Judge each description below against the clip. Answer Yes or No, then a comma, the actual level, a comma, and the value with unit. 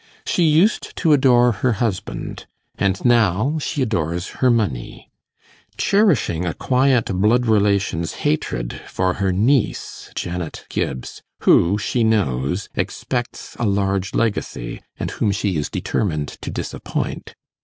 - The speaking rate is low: Yes, slow, 125 wpm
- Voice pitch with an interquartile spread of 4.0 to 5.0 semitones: No, wide, 5.5 semitones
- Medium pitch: No, low, 105 Hz